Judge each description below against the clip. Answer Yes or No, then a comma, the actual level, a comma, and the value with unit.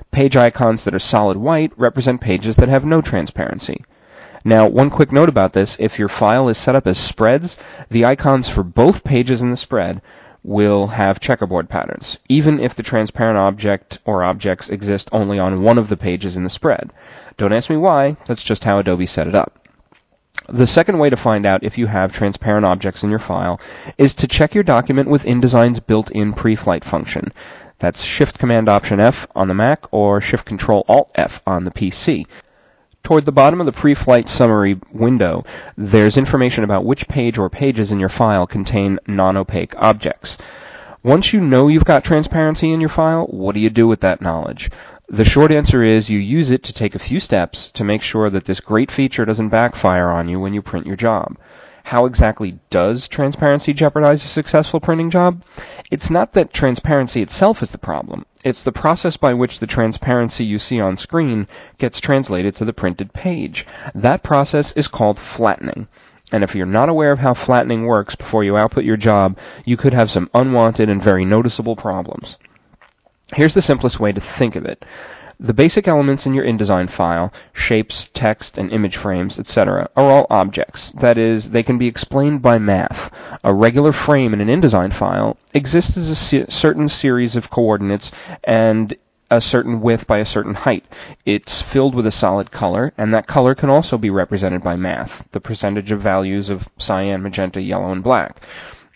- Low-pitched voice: Yes, low, 115 Hz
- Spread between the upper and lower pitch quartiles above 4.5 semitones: Yes, average, 5.2 semitones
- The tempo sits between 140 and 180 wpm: No, average, 190 wpm